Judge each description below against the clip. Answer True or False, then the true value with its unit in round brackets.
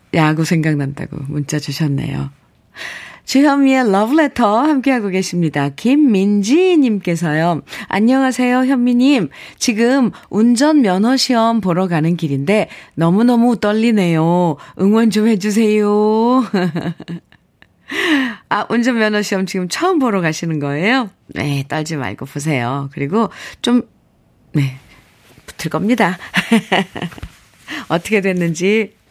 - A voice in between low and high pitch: False (200 Hz)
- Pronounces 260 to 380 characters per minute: False (240 characters per minute)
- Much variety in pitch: True (7.1 semitones)